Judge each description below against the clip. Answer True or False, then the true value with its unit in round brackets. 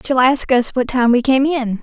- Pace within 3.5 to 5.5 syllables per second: True (4.9 syllables/s)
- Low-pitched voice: False (255 Hz)